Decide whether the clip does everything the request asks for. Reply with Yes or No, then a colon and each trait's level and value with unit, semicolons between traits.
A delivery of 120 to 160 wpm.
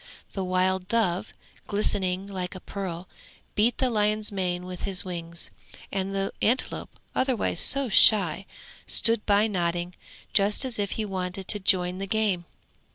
Yes: average, 150 wpm